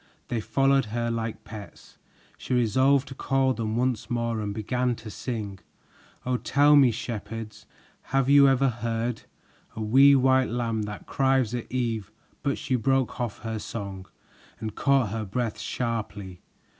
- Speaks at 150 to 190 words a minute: Yes, average, 155 wpm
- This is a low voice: Yes, low, 120 Hz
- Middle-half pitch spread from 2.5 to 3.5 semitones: Yes, average, 3.2 semitones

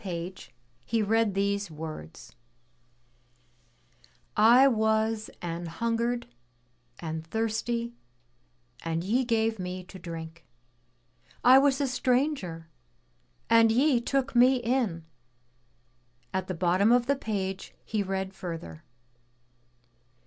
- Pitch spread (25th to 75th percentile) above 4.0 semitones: Yes, average, 5.1 semitones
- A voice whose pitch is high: Yes, high, 215 Hz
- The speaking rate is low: Yes, slow, 105 wpm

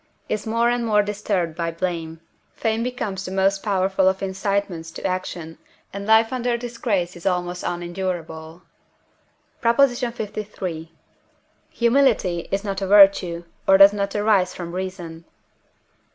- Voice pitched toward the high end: Yes, high, 195 Hz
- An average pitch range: Yes, average, 3.5 semitones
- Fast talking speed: No, slow, 135 wpm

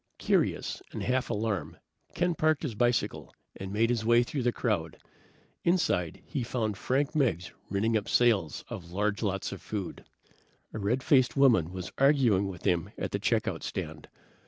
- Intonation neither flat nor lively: Yes, average, 4.8 semitones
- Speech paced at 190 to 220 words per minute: No, average, 170 wpm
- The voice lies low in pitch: Yes, low, 110 Hz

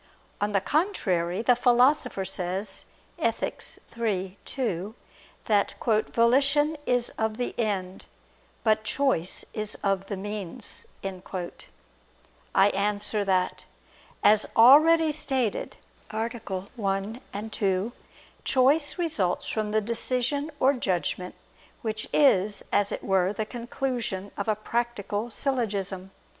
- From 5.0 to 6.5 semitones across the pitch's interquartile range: No, average, 4.1 semitones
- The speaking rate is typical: No, slow, 110 wpm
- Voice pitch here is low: No, high, 215 Hz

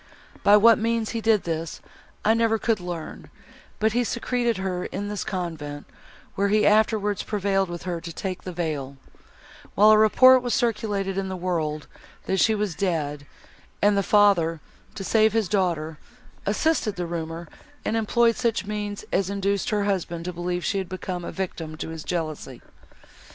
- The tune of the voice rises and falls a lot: No, average, 3.9 semitones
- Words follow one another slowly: No, average, 170 wpm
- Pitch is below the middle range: No, high, 195 Hz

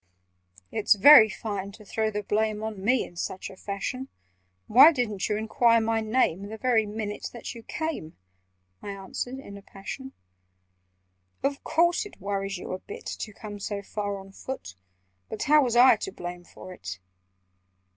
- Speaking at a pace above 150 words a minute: Yes, average, 170 wpm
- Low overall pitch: No, high, 215 Hz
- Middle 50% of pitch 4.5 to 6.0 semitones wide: No, average, 3.8 semitones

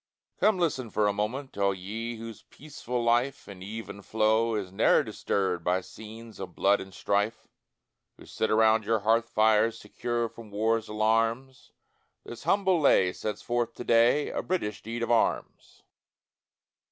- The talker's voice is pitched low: Yes, low, 110 Hz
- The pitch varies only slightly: Yes, narrow, 2.2 semitones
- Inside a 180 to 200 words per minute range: No, average, 155 wpm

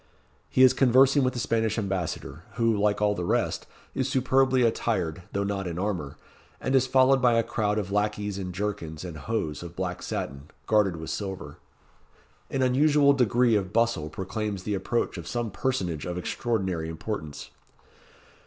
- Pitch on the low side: Yes, low, 105 Hz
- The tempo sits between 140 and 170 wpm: Yes, average, 165 wpm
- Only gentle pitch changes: No, average, 5.2 semitones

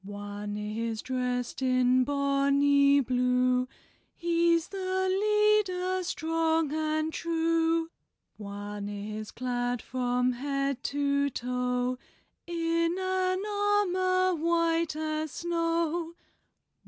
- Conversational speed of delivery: No, slow, 90 wpm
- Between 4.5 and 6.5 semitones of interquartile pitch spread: Yes, average, 5.2 semitones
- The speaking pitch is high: Yes, very high, 295 Hz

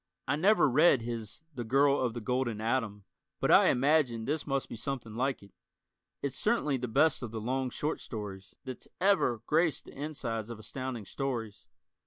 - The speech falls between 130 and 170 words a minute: No, average, 180 wpm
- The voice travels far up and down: No, average, 3.8 semitones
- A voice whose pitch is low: Yes, low, 130 Hz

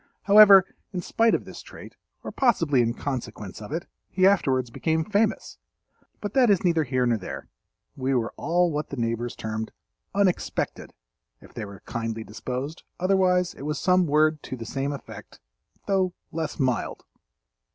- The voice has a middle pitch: Yes, medium, 150 Hz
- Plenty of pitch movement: Yes, wide, 7.1 semitones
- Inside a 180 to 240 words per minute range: No, average, 160 wpm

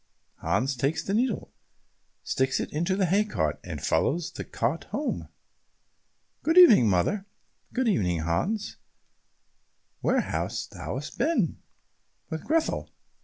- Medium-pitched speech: Yes, medium, 175 Hz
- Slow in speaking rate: Yes, slow, 120 wpm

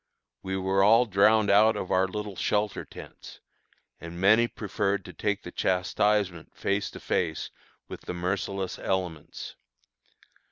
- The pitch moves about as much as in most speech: No, narrow, 2.2 semitones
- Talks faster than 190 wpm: No, slow, 135 wpm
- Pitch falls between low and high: No, low, 100 Hz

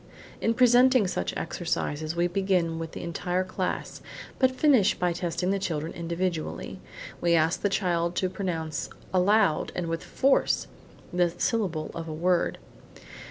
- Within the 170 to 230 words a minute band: No, average, 150 wpm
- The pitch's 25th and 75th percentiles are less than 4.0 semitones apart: Yes, average, 2.9 semitones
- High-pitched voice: No, medium, 180 Hz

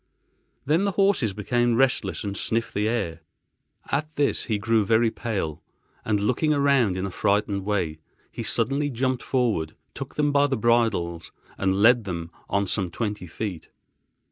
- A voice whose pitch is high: No, low, 110 Hz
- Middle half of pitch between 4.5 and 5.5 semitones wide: Yes, average, 4.9 semitones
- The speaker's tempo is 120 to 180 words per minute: Yes, average, 160 wpm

